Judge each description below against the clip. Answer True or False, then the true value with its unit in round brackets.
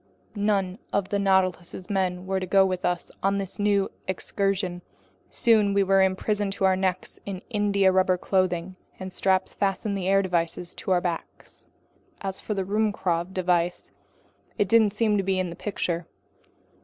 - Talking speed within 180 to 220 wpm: False (170 wpm)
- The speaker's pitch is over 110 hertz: True (190 Hz)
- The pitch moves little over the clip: True (1.5 semitones)